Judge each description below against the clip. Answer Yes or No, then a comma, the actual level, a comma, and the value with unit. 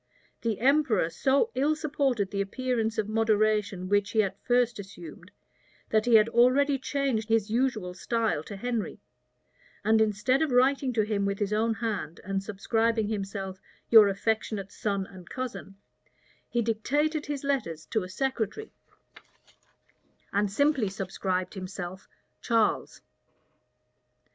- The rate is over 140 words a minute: No, slow, 135 wpm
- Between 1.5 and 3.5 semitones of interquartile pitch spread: No, average, 4.0 semitones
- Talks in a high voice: Yes, high, 220 Hz